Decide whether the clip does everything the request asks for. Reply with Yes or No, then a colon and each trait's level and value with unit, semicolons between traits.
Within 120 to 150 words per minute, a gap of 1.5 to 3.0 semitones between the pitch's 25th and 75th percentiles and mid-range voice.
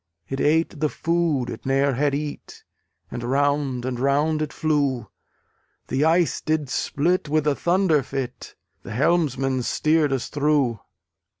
Yes: average, 140 wpm; narrow, 2.6 semitones; medium, 145 Hz